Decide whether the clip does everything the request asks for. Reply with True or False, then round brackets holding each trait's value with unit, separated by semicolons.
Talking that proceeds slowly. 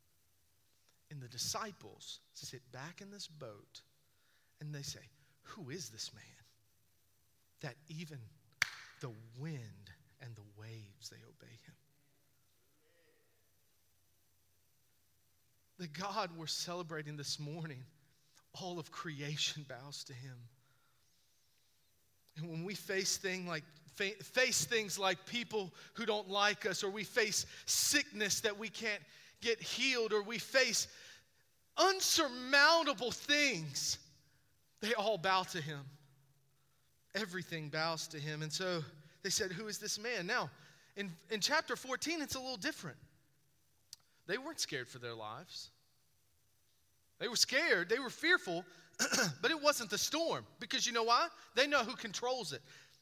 True (130 wpm)